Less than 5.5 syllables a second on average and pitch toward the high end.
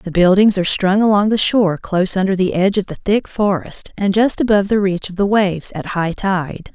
No: 5.6 syllables/s; high, 195 Hz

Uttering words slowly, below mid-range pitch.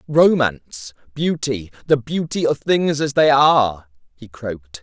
Yes: slow, 110 wpm; low, 130 Hz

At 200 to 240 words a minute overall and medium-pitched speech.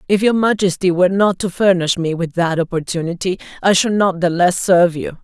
Yes: fast, 205 wpm; medium, 180 Hz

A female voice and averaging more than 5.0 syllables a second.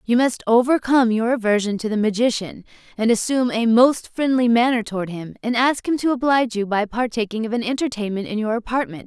Yes: female; 6.0 syllables/s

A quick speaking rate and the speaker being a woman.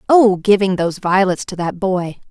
No: average, 180 wpm; female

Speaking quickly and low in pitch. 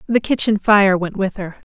No: fast, 210 wpm; high, 200 Hz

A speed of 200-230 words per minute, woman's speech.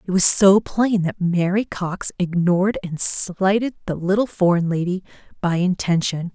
No: average, 150 wpm; female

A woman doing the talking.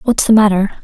Yes: female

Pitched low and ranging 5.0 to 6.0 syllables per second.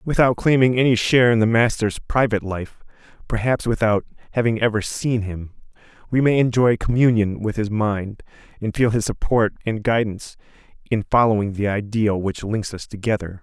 Yes: low, 110 Hz; 5.3 syllables/s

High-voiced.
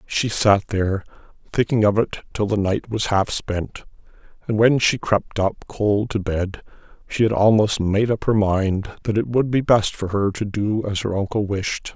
No: low, 105 Hz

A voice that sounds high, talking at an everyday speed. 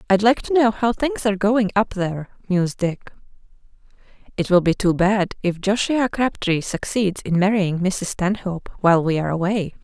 Yes: high, 195 Hz; average, 175 wpm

